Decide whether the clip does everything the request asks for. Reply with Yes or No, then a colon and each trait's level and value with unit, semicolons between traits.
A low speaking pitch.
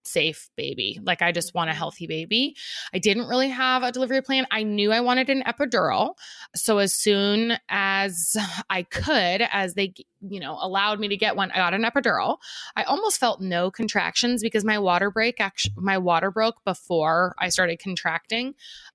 No: high, 200 Hz